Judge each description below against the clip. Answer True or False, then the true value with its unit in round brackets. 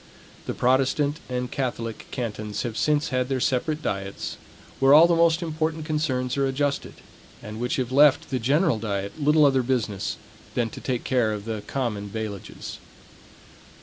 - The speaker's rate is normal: True (160 wpm)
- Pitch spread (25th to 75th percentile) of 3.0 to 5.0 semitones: True (4.6 semitones)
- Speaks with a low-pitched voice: True (130 Hz)